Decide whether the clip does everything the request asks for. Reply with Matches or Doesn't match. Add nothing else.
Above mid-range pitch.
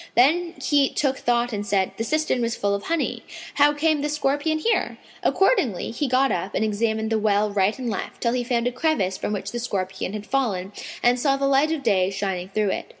Matches